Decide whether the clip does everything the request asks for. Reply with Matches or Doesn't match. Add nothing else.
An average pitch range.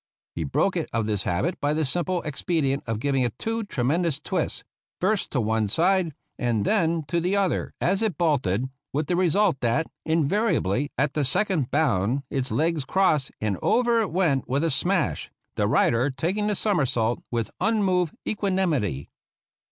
Doesn't match